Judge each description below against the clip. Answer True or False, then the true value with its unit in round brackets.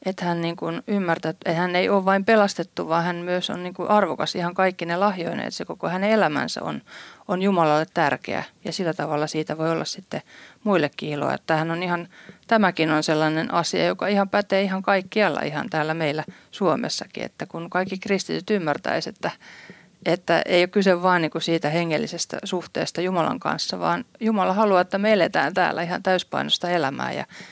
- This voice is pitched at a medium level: True (180 Hz)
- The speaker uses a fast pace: True (180 wpm)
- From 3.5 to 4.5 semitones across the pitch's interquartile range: False (2.8 semitones)